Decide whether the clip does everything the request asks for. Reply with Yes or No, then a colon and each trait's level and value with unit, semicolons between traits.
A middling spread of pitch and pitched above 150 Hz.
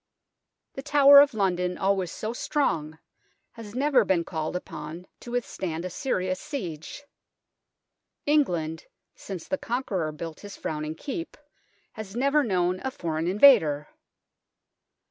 No: wide, 7.7 semitones; high, 190 Hz